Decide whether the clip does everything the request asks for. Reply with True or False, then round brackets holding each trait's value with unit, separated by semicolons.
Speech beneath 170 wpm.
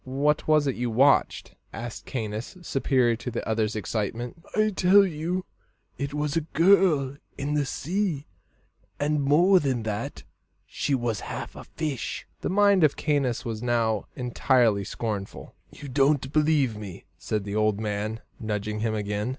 True (155 wpm)